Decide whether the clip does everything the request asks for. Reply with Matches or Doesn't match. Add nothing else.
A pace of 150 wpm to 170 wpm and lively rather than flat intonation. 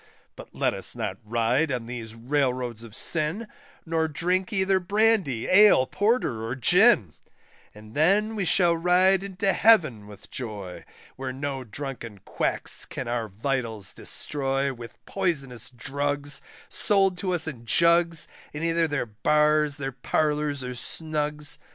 Doesn't match